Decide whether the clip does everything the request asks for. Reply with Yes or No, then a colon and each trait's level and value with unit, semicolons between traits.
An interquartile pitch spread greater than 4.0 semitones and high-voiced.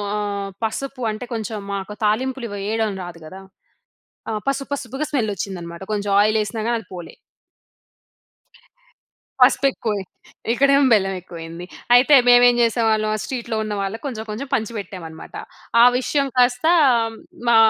No: average, 3.7 semitones; high, 220 Hz